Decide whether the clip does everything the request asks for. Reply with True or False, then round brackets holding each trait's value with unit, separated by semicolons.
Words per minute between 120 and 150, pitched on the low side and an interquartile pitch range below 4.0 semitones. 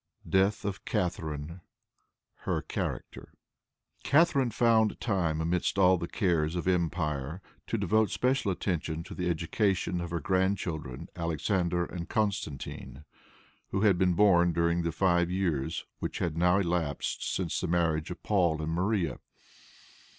True (135 wpm; 90 Hz; 2.8 semitones)